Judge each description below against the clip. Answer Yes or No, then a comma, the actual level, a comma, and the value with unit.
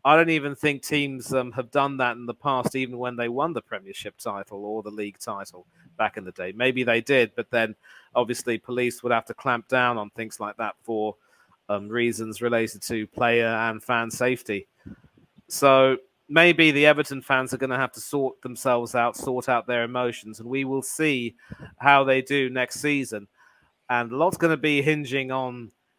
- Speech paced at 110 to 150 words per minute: No, average, 200 wpm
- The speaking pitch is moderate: No, low, 125 Hz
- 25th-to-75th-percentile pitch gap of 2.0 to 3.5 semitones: Yes, average, 3.0 semitones